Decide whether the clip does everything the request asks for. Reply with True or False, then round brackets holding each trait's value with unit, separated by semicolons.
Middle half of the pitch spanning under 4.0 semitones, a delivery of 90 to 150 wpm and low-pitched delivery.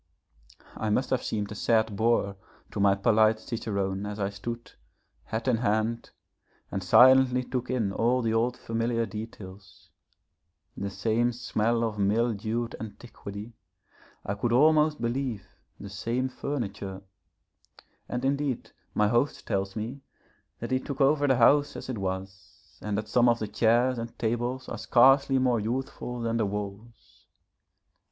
True (3.2 semitones; 145 wpm; 115 Hz)